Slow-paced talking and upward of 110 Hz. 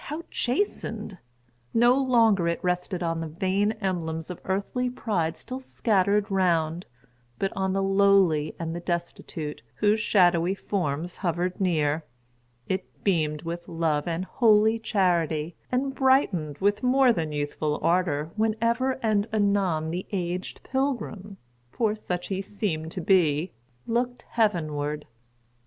Yes: slow, 125 wpm; medium, 185 Hz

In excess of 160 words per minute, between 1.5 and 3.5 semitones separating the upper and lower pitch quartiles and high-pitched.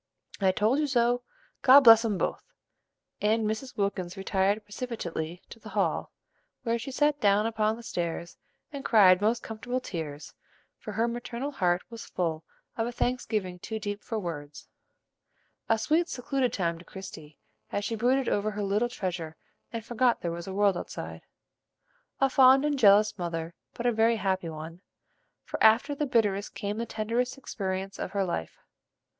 No: average, 170 wpm; average, 4.3 semitones; high, 215 Hz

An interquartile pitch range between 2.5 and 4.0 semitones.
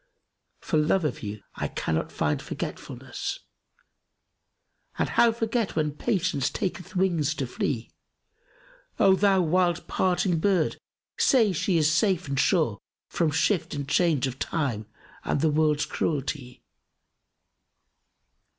No: average, 4.5 semitones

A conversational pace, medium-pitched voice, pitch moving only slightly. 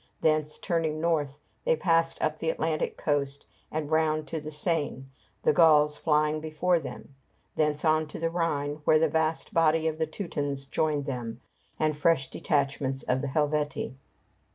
Yes: average, 160 wpm; medium, 155 Hz; narrow, 1.8 semitones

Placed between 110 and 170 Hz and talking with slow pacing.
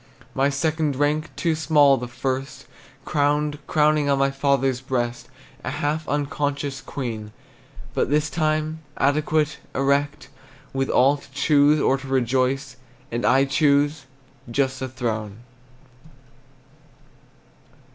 Yes: medium, 140 Hz; slow, 115 wpm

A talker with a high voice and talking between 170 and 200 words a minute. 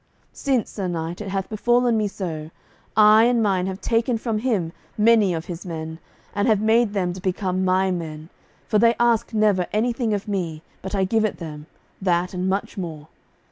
Yes: high, 195 Hz; average, 190 wpm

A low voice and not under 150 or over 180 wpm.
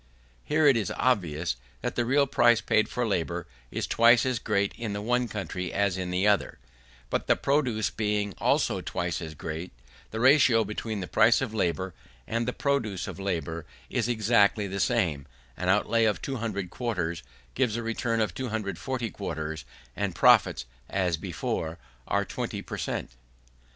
Yes: low, 105 Hz; average, 170 wpm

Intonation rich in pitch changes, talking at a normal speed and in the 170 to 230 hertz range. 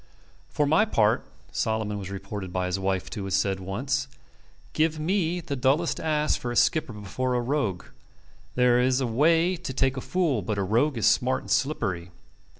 No: wide, 6.7 semitones; average, 185 wpm; low, 125 Hz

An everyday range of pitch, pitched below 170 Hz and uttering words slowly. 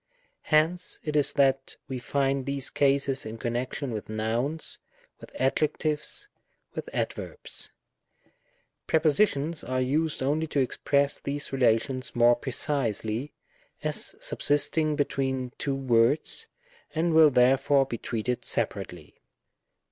Yes: average, 3.0 semitones; medium, 140 Hz; slow, 110 wpm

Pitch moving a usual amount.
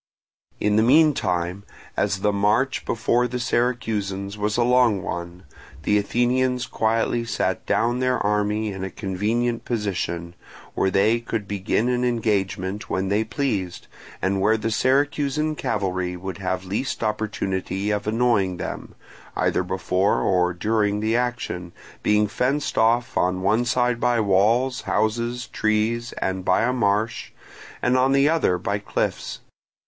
Yes: average, 3.9 semitones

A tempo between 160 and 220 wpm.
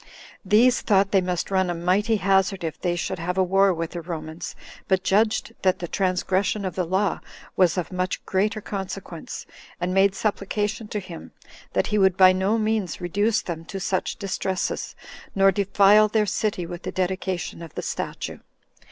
Yes: average, 180 wpm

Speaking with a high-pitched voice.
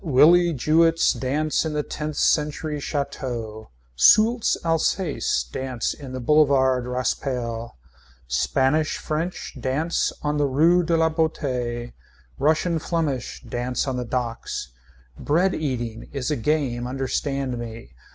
No: medium, 140 Hz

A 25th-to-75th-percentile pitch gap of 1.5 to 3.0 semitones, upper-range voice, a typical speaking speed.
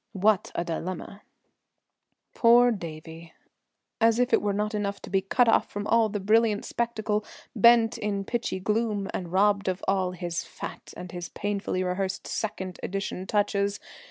Yes: average, 2.7 semitones; high, 200 Hz; average, 155 wpm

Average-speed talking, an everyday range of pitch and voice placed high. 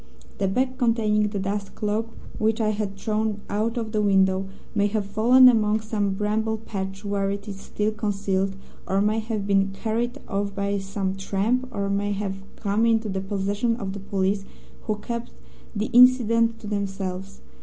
No: average, 175 wpm; narrow, 2.0 semitones; high, 205 Hz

